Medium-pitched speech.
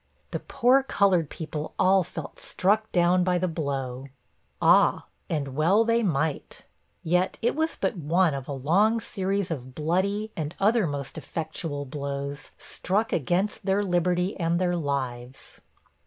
Yes: medium, 175 Hz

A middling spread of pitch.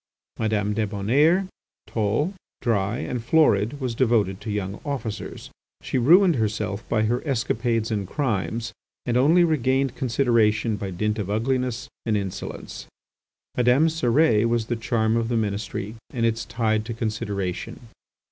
Yes: average, 3.0 semitones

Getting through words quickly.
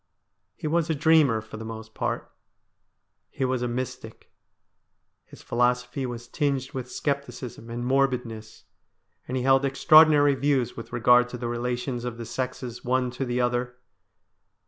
No: average, 155 wpm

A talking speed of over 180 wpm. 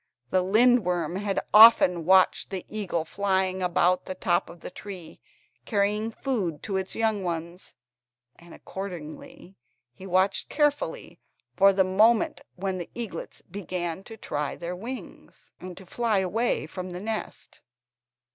No: average, 140 wpm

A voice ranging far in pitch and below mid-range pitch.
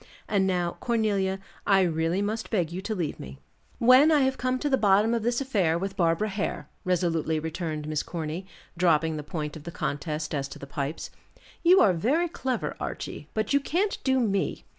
No: wide, 6.2 semitones; high, 190 Hz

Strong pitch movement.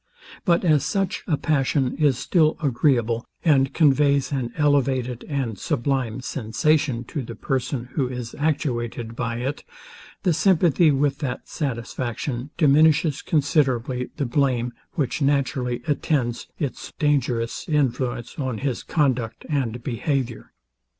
No: average, 3.5 semitones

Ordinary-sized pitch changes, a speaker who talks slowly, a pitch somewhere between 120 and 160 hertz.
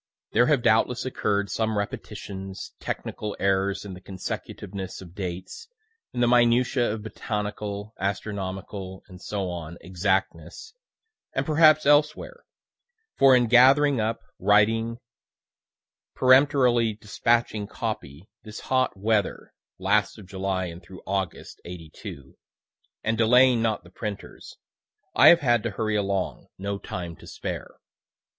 No: average, 3.8 semitones; slow, 120 wpm; low, 105 Hz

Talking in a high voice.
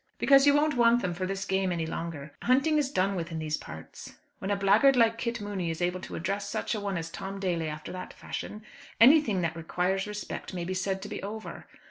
Yes: high, 195 Hz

